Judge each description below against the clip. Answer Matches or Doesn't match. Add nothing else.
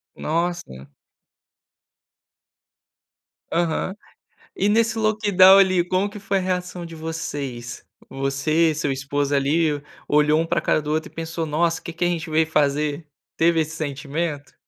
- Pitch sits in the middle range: Matches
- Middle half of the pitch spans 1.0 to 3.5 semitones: Matches